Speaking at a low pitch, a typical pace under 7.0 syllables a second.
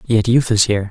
Yes: low, 110 Hz; 6.5 syllables/s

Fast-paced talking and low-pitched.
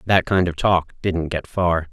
Yes: fast, 220 wpm; very low, 90 Hz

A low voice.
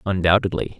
Yes: very low, 95 Hz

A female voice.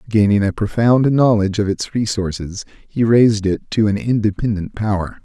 No: male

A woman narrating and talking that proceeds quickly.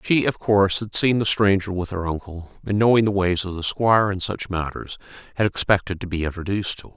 No: male; fast, 235 wpm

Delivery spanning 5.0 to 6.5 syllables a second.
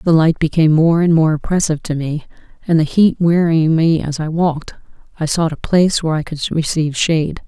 Yes: 6.0 syllables/s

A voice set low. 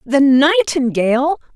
No: very high, 275 Hz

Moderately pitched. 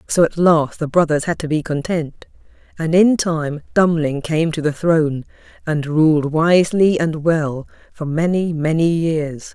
Yes: medium, 160 Hz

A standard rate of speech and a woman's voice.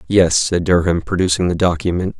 No: average, 165 wpm; male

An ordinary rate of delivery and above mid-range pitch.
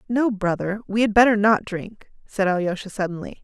Yes: average, 175 wpm; high, 205 Hz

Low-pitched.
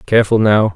Yes: low, 105 Hz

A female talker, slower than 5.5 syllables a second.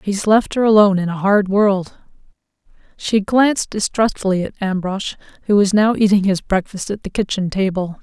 Yes: female; 5.1 syllables/s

